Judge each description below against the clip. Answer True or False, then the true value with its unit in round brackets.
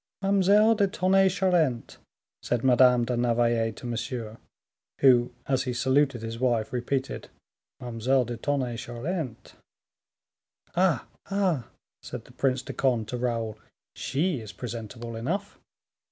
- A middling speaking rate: False (125 wpm)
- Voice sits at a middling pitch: False (125 Hz)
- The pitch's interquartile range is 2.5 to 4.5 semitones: False (4.9 semitones)